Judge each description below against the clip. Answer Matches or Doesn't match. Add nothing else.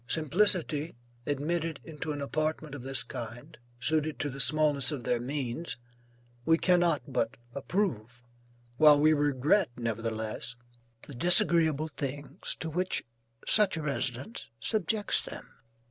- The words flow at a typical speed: Doesn't match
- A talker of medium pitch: Matches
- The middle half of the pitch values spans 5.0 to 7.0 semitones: Doesn't match